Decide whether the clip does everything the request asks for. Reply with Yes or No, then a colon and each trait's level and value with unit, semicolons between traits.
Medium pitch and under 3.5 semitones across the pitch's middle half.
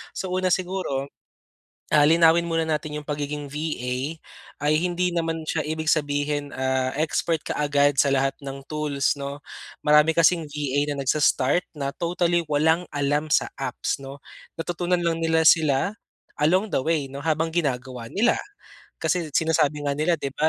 Yes: medium, 150 Hz; narrow, 2.6 semitones